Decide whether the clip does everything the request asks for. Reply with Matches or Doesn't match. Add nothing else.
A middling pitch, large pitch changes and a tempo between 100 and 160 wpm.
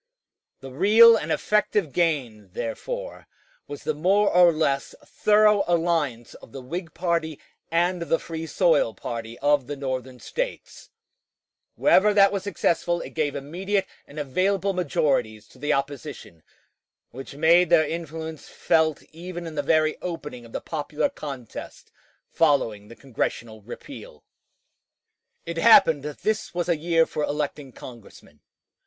Doesn't match